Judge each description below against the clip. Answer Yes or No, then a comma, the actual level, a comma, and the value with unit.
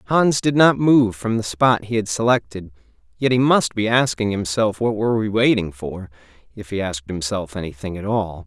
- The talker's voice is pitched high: No, low, 105 Hz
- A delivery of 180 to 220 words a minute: Yes, average, 200 wpm